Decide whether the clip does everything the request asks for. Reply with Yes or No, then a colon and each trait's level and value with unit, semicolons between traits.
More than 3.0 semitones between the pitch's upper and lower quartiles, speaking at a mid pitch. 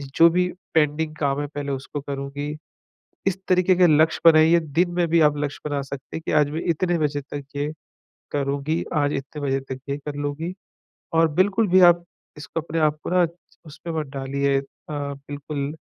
No: average, 2.7 semitones; medium, 150 Hz